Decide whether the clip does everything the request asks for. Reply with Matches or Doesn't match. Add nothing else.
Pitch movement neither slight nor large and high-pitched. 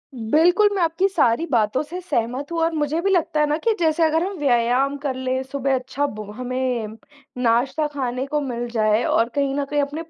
Matches